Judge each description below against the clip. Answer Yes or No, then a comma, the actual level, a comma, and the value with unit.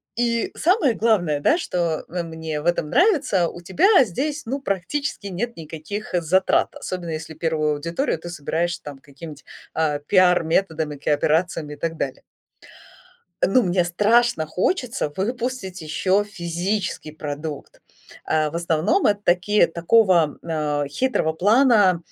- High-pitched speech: No, medium, 175 Hz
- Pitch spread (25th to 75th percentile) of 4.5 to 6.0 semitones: Yes, average, 5.3 semitones